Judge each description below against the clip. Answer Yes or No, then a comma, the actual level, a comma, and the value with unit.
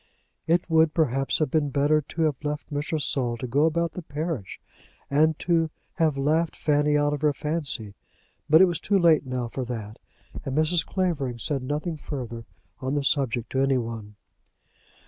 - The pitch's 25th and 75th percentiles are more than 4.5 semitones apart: No, average, 3.4 semitones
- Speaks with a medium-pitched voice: Yes, medium, 145 Hz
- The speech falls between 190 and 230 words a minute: No, average, 180 wpm